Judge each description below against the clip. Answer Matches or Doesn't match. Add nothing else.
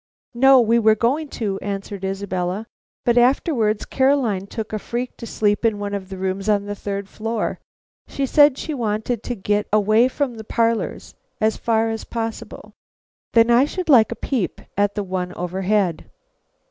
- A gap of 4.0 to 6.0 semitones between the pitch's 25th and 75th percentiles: Doesn't match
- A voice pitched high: Matches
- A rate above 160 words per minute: Matches